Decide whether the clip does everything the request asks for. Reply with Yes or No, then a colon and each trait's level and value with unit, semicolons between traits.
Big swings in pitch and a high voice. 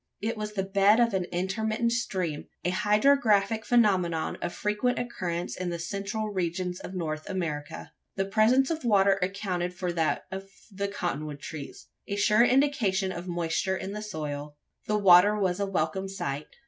No: average, 3.3 semitones; high, 195 Hz